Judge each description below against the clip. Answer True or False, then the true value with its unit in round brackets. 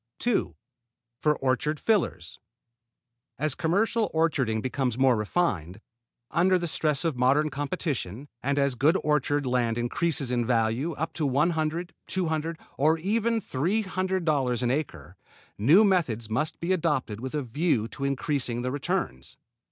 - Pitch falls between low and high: True (145 Hz)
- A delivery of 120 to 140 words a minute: False (150 wpm)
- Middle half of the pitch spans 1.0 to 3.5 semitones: False (5.2 semitones)